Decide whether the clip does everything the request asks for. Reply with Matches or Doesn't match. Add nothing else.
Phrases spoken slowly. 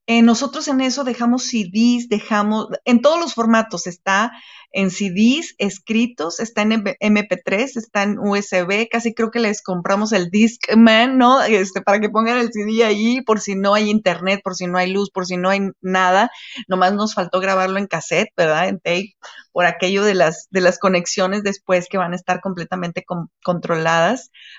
Doesn't match